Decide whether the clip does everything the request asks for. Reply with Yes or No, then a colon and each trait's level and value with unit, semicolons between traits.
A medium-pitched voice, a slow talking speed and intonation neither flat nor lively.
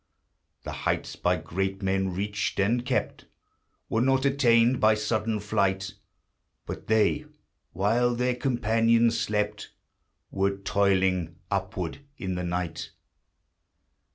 No: low, 105 Hz; slow, 110 wpm; average, 3.4 semitones